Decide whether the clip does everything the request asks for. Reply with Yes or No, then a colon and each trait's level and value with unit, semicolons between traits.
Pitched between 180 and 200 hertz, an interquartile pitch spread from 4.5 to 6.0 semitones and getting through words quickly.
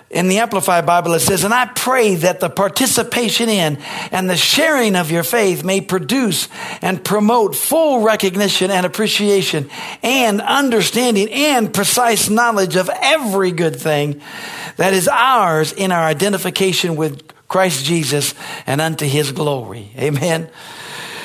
No: high, 190 Hz; average, 5.1 semitones; average, 140 wpm